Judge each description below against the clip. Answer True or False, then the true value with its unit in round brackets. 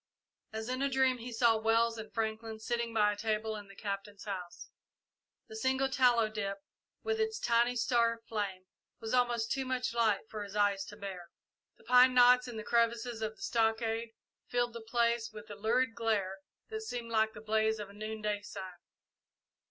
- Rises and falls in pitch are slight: True (2.2 semitones)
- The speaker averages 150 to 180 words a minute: False (190 wpm)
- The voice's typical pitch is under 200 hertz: False (225 Hz)